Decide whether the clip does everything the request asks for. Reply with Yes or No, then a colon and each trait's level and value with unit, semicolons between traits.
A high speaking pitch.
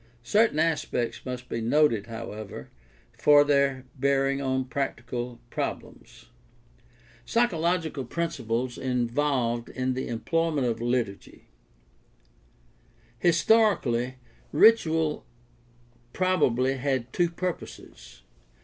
No: low, 130 Hz